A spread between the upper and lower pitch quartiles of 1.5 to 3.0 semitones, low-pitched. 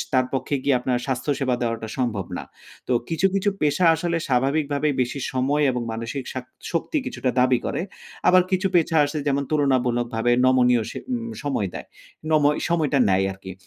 No: average, 3.6 semitones; low, 130 Hz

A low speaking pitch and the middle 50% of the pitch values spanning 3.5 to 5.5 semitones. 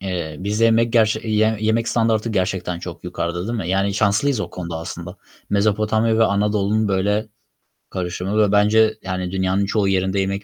No: low, 100 Hz; average, 2.8 semitones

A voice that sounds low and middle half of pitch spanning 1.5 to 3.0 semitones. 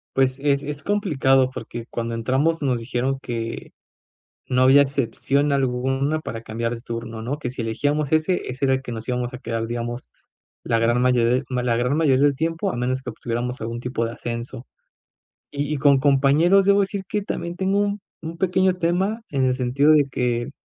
No: low, 130 Hz; average, 3.7 semitones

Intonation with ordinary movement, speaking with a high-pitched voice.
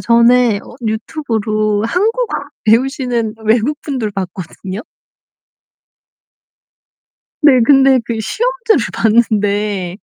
Yes: average, 4.2 semitones; high, 230 Hz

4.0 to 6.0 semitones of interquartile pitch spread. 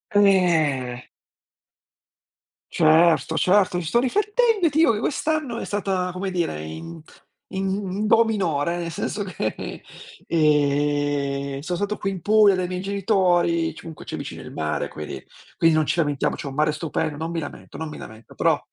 Yes: average, 5.2 semitones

